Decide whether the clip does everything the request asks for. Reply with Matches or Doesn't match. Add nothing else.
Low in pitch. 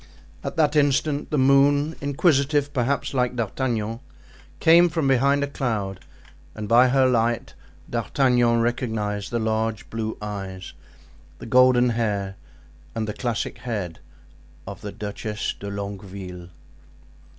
Matches